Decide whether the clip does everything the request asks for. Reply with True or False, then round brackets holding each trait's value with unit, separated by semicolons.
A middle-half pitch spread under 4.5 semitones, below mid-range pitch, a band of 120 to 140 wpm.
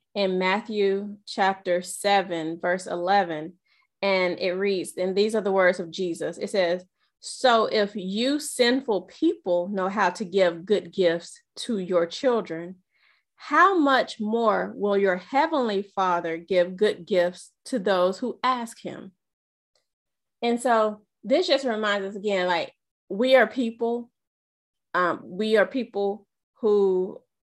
False (4.0 semitones; 200 Hz; 135 wpm)